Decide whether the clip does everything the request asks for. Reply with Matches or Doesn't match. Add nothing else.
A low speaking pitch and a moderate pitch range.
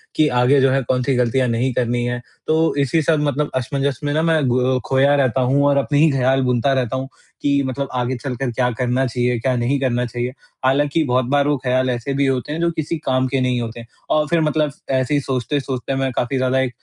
Doesn't match